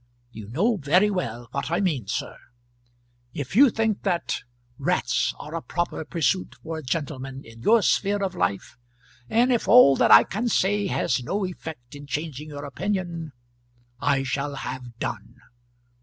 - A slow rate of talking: No, average, 160 wpm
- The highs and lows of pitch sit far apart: Yes, wide, 6.3 semitones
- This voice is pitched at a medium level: Yes, medium, 155 Hz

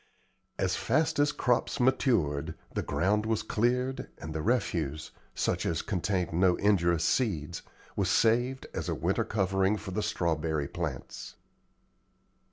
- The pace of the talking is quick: No, slow, 135 wpm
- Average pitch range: No, wide, 6.3 semitones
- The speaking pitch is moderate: No, very low, 95 Hz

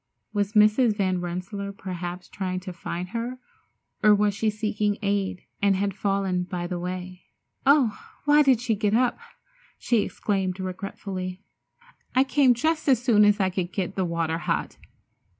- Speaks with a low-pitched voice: No, high, 200 Hz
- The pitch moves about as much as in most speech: Yes, average, 3.0 semitones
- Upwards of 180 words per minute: No, average, 160 wpm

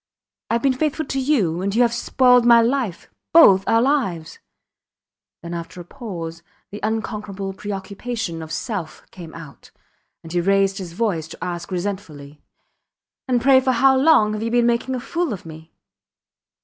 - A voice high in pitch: Yes, high, 205 Hz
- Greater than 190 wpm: No, average, 165 wpm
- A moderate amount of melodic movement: No, wide, 6.1 semitones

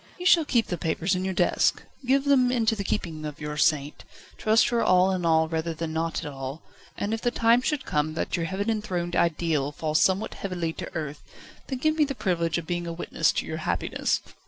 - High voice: No, medium, 175 Hz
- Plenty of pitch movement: Yes, wide, 5.8 semitones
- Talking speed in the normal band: No, fast, 225 wpm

